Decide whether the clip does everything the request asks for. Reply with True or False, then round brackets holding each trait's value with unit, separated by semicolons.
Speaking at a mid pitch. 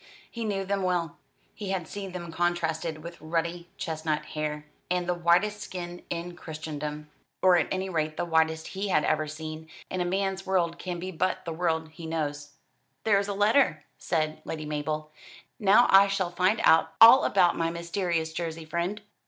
True (170 Hz)